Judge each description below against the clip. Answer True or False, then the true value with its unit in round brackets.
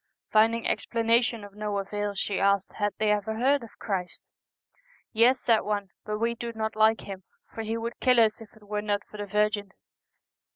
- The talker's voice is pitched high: True (215 Hz)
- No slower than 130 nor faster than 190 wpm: False (205 wpm)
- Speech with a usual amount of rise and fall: False (1.9 semitones)